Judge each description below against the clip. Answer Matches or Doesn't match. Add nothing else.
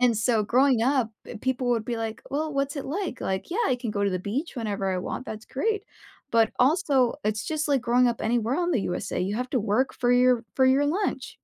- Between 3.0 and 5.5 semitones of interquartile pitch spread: Matches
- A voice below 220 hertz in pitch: Doesn't match